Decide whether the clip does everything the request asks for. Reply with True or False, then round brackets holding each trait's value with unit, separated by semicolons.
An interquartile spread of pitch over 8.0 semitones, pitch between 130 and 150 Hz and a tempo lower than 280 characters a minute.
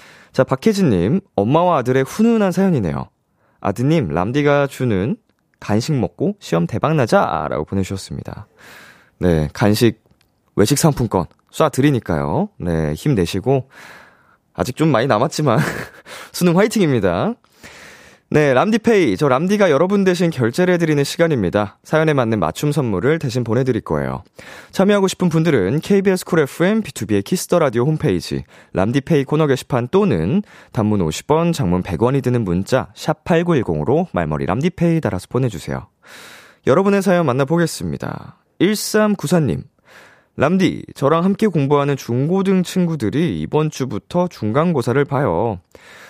False (8.8 semitones; 140 Hz; 310 characters per minute)